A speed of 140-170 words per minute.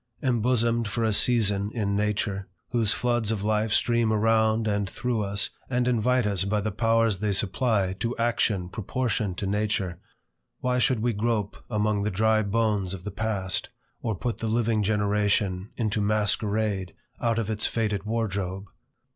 Yes: average, 160 wpm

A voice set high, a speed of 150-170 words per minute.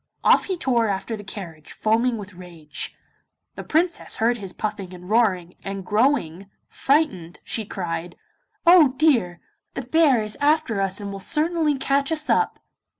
Yes: high, 215 Hz; average, 155 wpm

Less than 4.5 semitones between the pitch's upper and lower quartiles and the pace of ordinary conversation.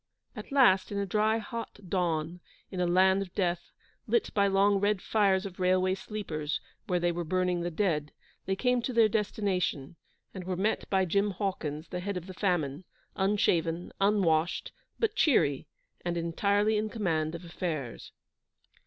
Yes: average, 3.0 semitones; average, 165 wpm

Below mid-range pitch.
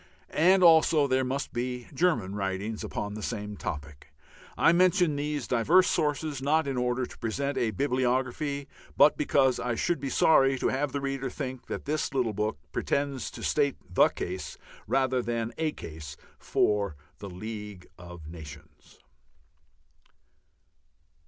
Yes: low, 130 Hz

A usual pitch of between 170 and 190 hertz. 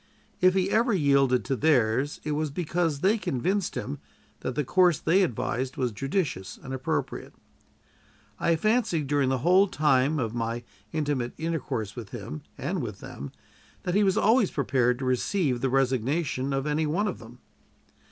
No: medium, 140 Hz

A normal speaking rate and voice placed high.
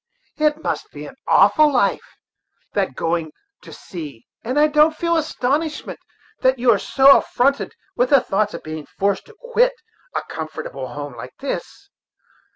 Yes: average, 160 wpm; very high, 255 Hz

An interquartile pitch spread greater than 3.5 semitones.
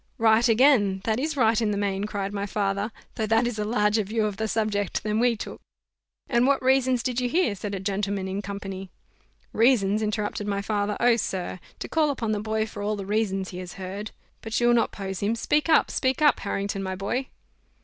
No: average, 2.9 semitones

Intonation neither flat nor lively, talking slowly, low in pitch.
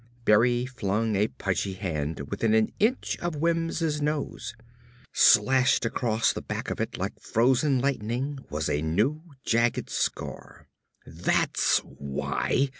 No: wide, 5.9 semitones; slow, 125 wpm; low, 115 Hz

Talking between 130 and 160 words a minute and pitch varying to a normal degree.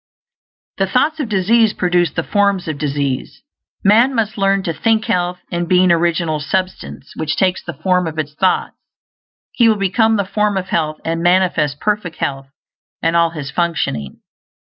No: average, 170 wpm; average, 4.1 semitones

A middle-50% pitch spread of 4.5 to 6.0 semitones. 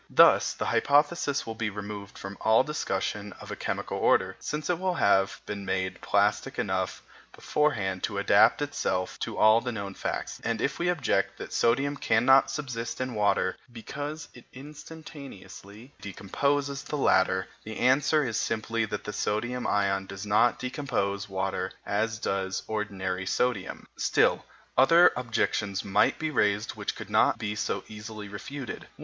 Yes: wide, 5.6 semitones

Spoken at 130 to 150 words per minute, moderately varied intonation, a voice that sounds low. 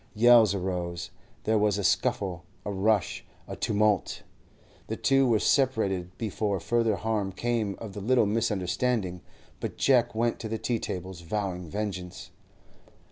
Yes: average, 140 wpm; average, 3.4 semitones; low, 105 Hz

